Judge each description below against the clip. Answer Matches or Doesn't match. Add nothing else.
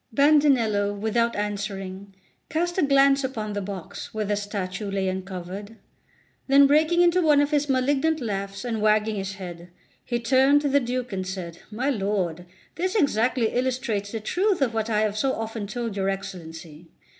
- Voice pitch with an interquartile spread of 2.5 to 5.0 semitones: Doesn't match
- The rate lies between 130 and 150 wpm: Doesn't match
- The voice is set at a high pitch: Matches